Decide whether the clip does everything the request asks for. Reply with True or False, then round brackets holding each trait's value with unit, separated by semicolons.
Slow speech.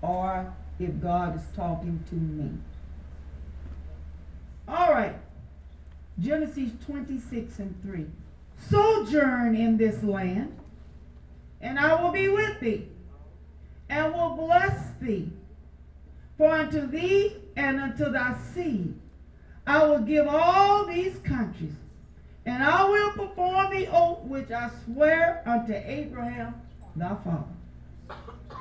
True (110 wpm)